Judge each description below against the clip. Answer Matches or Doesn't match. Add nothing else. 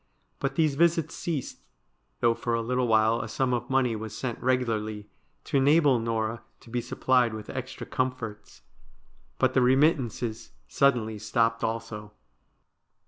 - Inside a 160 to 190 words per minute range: Doesn't match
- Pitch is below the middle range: Matches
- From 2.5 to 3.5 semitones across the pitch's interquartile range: Matches